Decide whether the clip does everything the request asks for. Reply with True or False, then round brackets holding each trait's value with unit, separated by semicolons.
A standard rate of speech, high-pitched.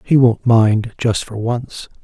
False (175 wpm; 115 Hz)